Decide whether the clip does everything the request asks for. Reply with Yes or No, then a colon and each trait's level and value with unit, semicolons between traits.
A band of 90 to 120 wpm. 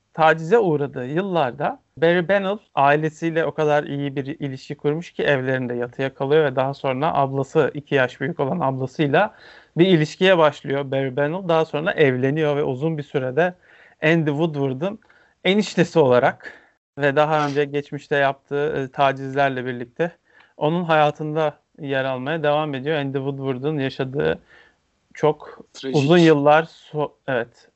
No: average, 135 wpm